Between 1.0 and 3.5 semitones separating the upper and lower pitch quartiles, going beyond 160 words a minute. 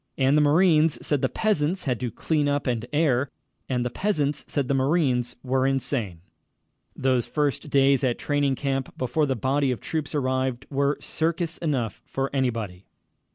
Yes: narrow, 2.6 semitones; average, 170 wpm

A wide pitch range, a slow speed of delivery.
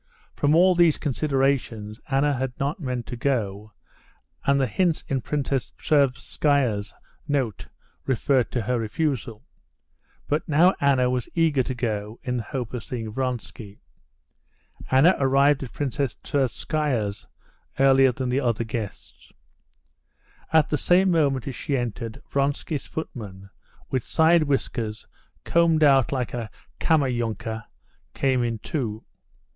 No: average, 3.7 semitones; slow, 130 wpm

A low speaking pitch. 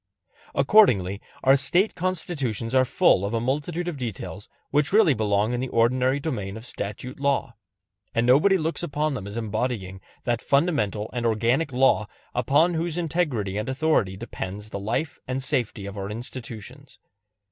Yes: low, 125 Hz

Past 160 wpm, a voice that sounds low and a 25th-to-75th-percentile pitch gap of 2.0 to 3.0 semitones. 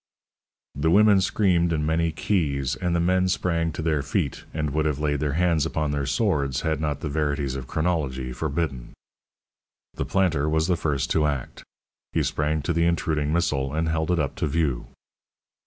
Yes: average, 185 wpm; very low, 80 Hz; average, 2.7 semitones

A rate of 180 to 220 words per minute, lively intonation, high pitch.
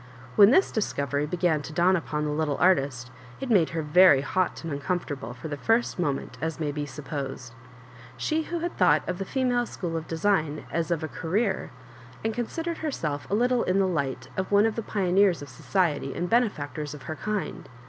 No: average, 200 wpm; wide, 5.8 semitones; medium, 170 Hz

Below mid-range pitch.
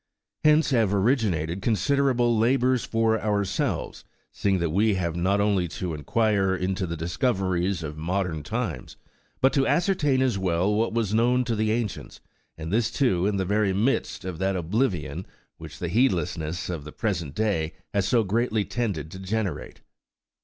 Yes: low, 100 Hz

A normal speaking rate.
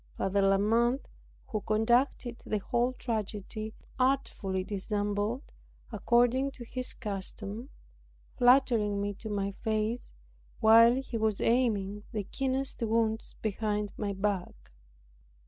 No: slow, 110 wpm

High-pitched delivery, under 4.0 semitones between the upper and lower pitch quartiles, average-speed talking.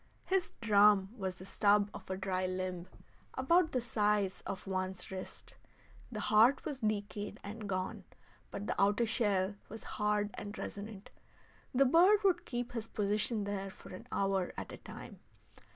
Yes: high, 205 Hz; average, 3.1 semitones; average, 160 wpm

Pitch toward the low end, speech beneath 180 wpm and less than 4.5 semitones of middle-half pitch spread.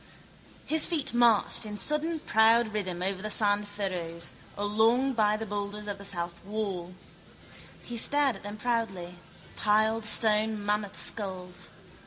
No: high, 210 Hz; average, 140 wpm; narrow, 2.4 semitones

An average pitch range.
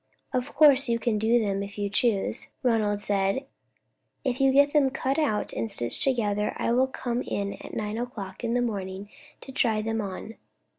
Yes: average, 4.0 semitones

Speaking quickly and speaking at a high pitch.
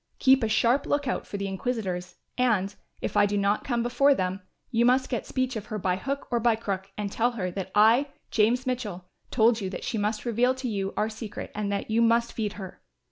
Yes: fast, 230 wpm; high, 220 Hz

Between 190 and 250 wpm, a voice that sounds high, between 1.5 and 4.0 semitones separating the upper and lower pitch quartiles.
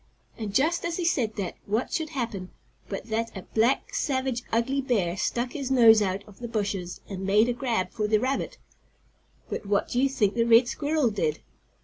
No: average, 200 wpm; high, 230 Hz; average, 4.5 semitones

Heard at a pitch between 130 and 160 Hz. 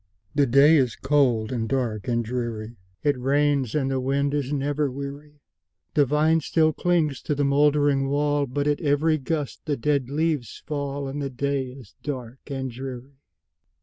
Yes: medium, 140 Hz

